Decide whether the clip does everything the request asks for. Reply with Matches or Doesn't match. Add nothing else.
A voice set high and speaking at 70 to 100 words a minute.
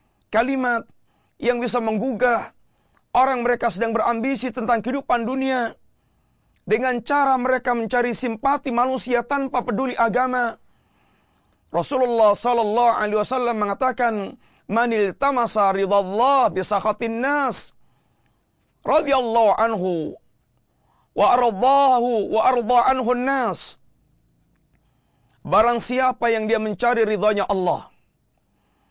Matches